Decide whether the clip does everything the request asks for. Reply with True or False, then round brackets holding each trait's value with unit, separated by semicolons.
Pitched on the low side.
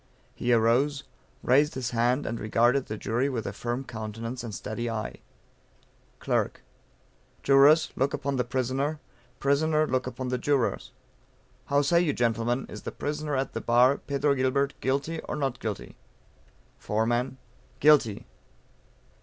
True (130 Hz)